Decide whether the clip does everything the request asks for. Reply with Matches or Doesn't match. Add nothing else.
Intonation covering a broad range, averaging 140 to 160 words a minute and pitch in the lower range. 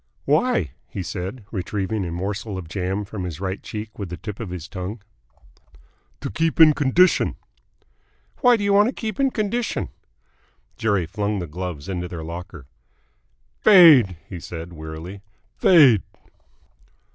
Matches